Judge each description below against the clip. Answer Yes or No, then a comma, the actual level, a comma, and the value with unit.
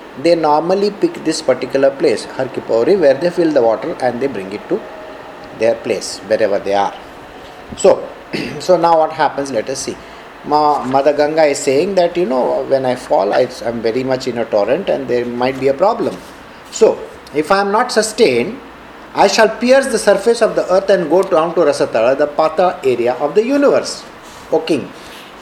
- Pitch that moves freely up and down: Yes, wide, 7.0 semitones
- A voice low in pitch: No, medium, 155 Hz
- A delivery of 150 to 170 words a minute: No, average, 185 wpm